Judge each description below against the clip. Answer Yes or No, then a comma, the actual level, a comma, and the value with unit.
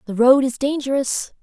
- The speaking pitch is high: Yes, very high, 260 Hz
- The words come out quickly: No, average, 170 wpm